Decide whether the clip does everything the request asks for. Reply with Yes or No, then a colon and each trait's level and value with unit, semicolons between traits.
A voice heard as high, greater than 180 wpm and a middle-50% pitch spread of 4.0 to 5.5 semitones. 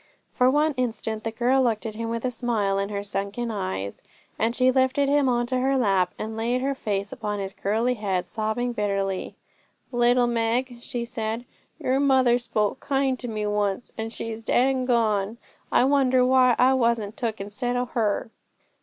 No: high, 235 Hz; average, 190 wpm; average, 3.2 semitones